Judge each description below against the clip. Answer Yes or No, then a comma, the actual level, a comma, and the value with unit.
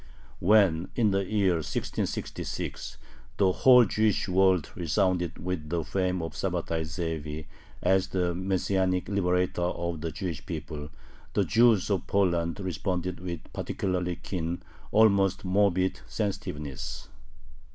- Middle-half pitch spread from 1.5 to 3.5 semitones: Yes, narrow, 2.6 semitones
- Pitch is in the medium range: No, very low, 90 Hz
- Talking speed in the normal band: No, slow, 120 wpm